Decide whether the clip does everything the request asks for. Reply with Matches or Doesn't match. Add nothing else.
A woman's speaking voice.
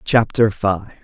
Doesn't match